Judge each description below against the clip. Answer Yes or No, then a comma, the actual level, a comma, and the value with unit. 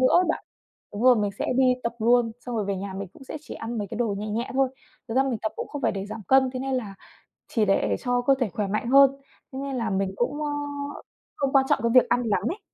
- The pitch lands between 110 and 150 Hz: No, high, 235 Hz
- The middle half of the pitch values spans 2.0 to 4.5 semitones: Yes, average, 4.1 semitones